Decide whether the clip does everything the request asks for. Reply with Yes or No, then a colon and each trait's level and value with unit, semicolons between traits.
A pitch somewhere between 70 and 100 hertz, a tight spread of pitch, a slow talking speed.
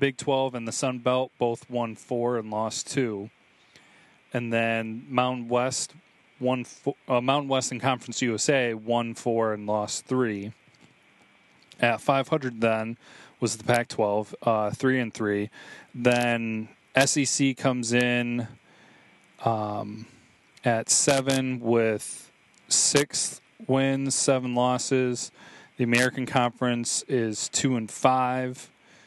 No: low, 125 Hz; narrow, 2.3 semitones; slow, 120 wpm